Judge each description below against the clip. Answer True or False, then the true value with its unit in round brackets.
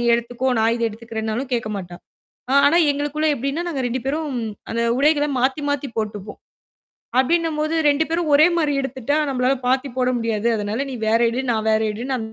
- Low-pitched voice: False (260 Hz)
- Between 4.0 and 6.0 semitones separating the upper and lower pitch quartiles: True (4.3 semitones)